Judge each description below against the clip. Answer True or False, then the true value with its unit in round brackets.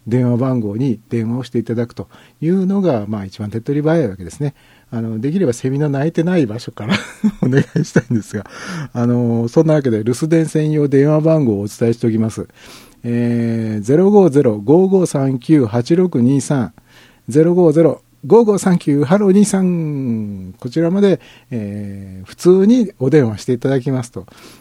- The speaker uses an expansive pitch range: True (5.9 semitones)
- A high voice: False (135 Hz)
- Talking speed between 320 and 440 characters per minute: False (280 characters per minute)